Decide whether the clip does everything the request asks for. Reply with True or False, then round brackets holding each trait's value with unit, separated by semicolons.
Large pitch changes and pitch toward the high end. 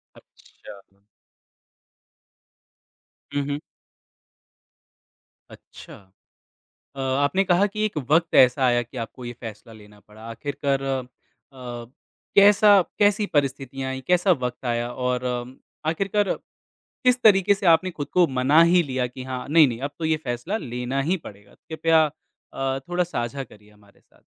False (5.8 semitones; 135 Hz)